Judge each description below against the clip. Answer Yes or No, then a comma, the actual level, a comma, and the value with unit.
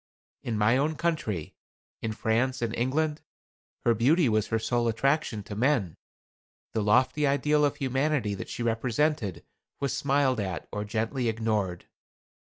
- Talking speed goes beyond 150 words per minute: No, average, 145 wpm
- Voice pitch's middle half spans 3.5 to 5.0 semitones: Yes, average, 4.5 semitones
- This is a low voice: Yes, low, 120 Hz